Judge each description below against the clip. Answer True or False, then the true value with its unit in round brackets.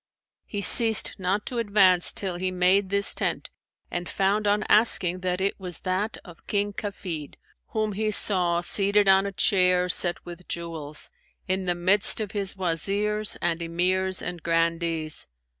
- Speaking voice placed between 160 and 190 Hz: True (185 Hz)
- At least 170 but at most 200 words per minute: False (160 wpm)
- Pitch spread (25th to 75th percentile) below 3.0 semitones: True (2.6 semitones)